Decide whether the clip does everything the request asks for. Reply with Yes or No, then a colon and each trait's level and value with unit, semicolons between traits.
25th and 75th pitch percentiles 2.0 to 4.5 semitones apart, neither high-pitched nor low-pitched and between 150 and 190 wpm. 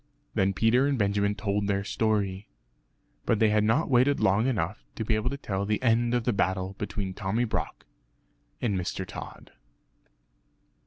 No: average, 2.8 semitones; low, 105 Hz; average, 165 wpm